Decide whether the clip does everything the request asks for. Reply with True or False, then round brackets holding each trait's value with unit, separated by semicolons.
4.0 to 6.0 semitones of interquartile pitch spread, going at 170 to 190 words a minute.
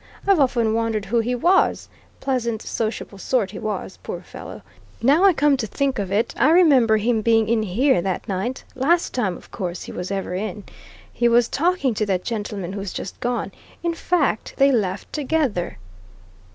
True (5.1 semitones; 180 wpm)